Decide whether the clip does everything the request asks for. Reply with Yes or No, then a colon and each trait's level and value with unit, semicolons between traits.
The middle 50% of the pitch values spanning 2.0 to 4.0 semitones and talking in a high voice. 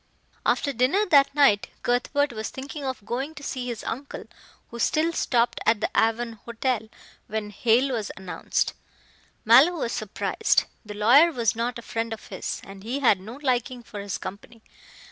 Yes: average, 3.7 semitones; high, 235 Hz